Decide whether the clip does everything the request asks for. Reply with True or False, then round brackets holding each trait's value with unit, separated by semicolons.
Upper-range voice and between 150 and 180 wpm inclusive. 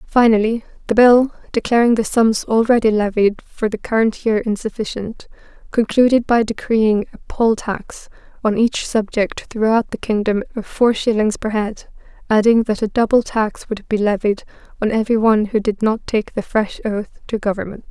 True (220 Hz; 170 wpm)